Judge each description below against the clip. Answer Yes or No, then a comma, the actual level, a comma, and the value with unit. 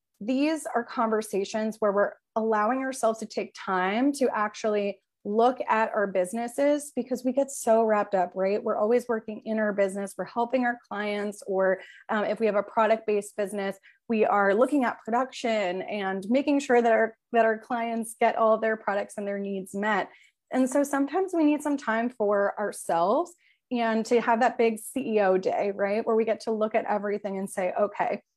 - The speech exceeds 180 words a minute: Yes, average, 190 wpm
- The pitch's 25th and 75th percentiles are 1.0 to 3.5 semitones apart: Yes, average, 2.8 semitones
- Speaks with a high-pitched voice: Yes, high, 220 Hz